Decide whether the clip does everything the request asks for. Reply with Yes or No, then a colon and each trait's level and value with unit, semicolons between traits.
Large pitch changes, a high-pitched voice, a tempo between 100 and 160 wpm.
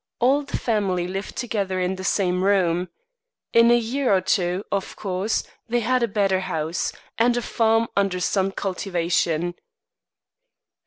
No: average, 3.9 semitones; high, 195 Hz; average, 150 wpm